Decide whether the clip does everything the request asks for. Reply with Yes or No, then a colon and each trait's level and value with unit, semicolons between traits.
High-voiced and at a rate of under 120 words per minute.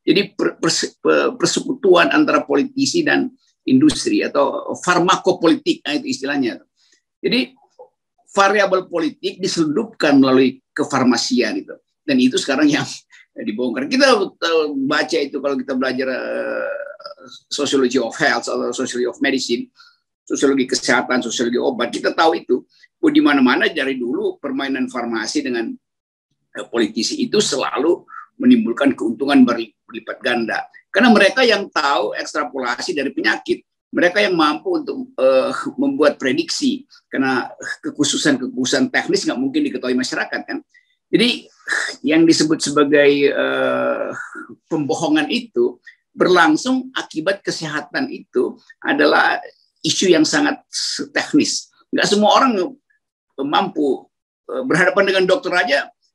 Yes: very high, 265 Hz; average, 110 wpm